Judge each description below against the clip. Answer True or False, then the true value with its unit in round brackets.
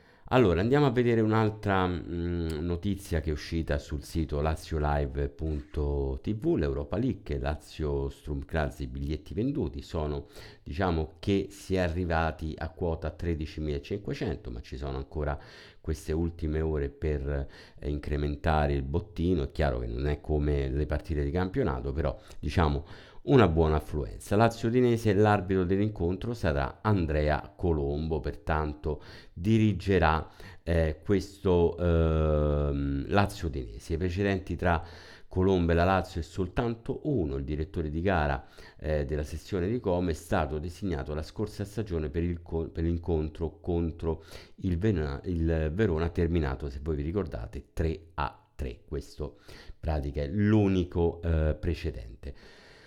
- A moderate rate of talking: True (135 wpm)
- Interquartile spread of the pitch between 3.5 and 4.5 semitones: True (4.1 semitones)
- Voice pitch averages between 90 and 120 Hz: False (80 Hz)